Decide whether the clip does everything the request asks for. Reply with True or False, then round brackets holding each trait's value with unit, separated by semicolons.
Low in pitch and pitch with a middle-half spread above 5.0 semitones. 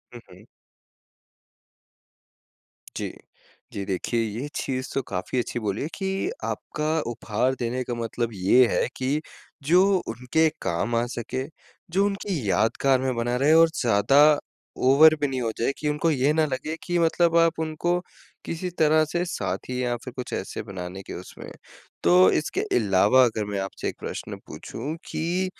True (130 Hz; 5.5 semitones)